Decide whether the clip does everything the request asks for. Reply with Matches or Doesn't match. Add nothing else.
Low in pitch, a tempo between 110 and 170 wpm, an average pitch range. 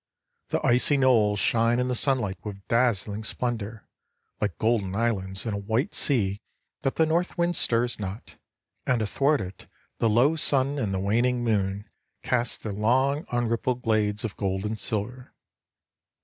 Matches